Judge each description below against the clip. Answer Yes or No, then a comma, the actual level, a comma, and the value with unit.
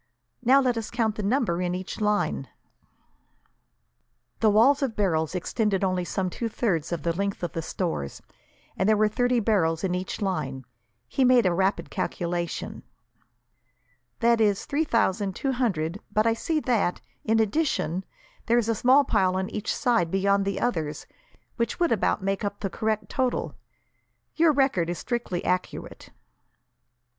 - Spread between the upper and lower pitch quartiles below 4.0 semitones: No, average, 4.5 semitones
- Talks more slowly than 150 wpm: No, average, 160 wpm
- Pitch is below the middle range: No, high, 205 Hz